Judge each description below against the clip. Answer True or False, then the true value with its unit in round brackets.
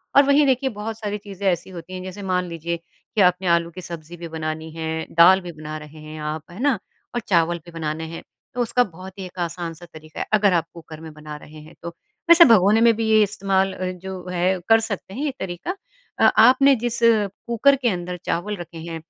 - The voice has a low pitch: False (180 Hz)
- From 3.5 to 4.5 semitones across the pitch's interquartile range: True (4.1 semitones)